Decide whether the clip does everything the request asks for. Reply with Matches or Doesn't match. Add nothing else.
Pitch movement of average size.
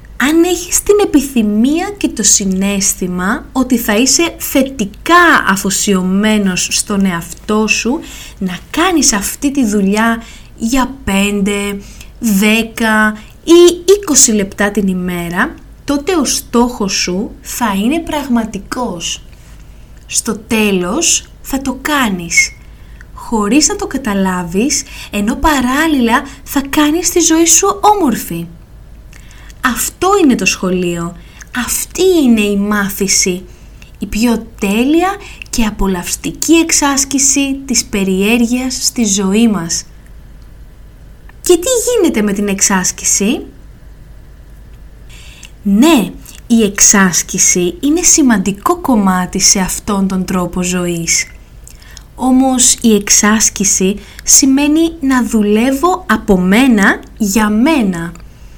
Doesn't match